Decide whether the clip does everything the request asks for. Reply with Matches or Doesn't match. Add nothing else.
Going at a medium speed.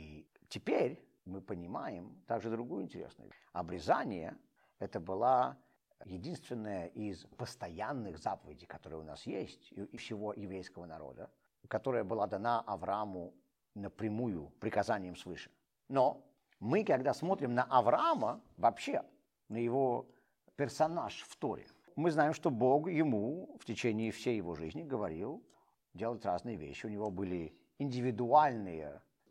Matches